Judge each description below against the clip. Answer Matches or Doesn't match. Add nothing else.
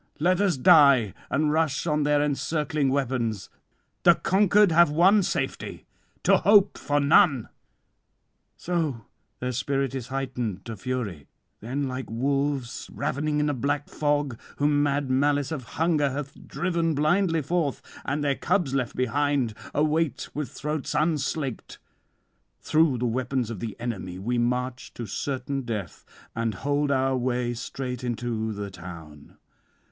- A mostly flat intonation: Doesn't match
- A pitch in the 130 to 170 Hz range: Matches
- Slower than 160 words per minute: Matches